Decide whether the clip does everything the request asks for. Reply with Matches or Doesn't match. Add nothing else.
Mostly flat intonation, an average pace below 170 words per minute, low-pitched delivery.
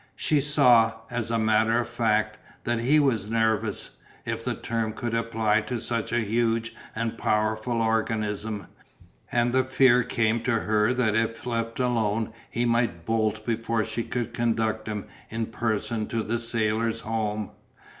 Matches